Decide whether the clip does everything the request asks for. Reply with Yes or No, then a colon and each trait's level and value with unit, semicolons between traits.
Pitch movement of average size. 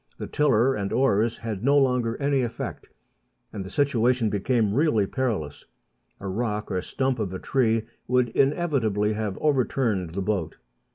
Yes: average, 4.3 semitones